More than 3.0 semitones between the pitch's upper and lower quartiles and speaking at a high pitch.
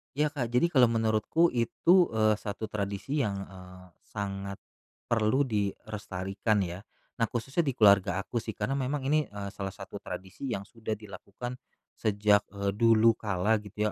No: average, 3.4 semitones; low, 110 Hz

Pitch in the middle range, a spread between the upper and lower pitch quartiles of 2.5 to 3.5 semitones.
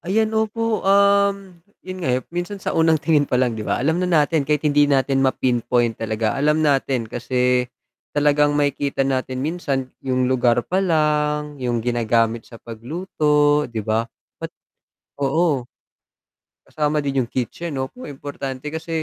No: medium, 145 Hz; average, 4.2 semitones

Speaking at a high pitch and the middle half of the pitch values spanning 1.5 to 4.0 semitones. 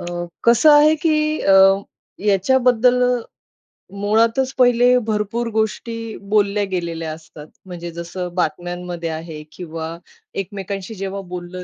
No: high, 195 Hz; average, 5.2 semitones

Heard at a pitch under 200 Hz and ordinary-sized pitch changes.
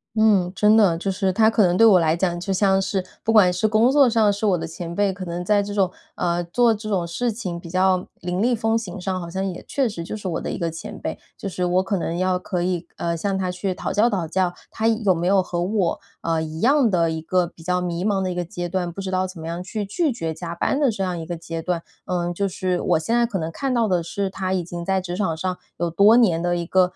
Yes: medium, 185 Hz; average, 3.0 semitones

